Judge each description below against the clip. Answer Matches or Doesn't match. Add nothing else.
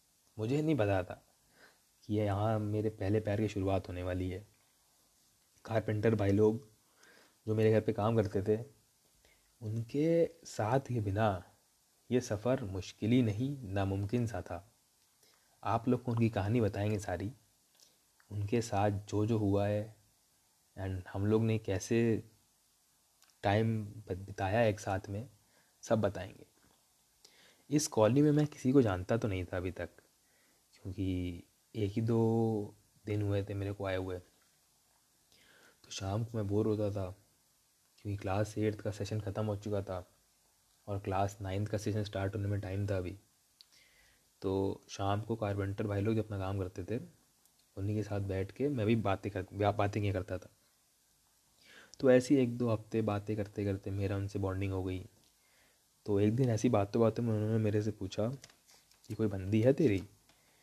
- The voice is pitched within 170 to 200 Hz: Doesn't match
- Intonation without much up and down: Matches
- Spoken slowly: Doesn't match